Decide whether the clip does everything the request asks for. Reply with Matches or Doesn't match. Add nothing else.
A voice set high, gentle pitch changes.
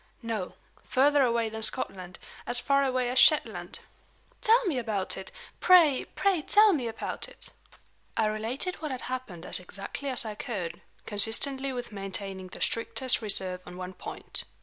Doesn't match